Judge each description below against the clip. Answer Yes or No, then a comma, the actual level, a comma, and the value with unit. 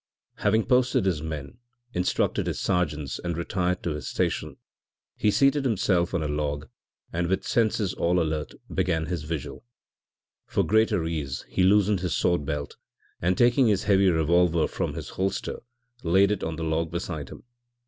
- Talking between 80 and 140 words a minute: No, average, 165 wpm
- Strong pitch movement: No, average, 3.9 semitones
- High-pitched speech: No, very low, 90 Hz